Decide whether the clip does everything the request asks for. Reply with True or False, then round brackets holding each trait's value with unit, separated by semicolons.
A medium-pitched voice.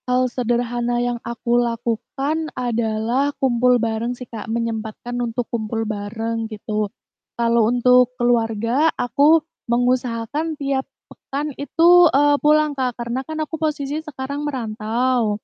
False (245 Hz)